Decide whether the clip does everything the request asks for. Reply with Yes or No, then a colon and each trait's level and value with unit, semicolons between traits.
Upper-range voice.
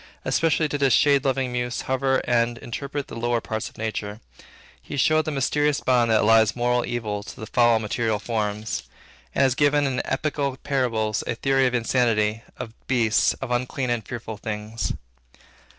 No: low, 120 Hz